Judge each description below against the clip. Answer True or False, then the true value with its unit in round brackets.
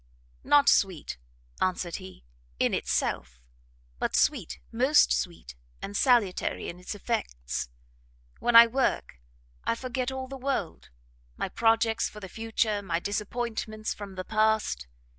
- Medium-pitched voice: False (215 Hz)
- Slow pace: True (130 wpm)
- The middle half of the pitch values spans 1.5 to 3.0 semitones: False (4.4 semitones)